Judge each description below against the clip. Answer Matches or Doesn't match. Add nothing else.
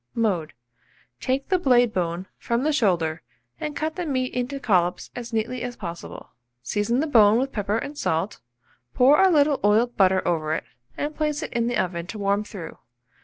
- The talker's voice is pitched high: Matches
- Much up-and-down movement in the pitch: Matches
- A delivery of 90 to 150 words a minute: Doesn't match